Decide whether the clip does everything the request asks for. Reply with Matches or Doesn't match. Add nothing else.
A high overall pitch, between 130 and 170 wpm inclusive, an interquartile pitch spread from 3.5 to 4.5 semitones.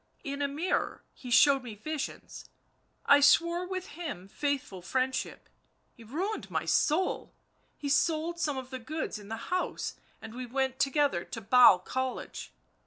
Matches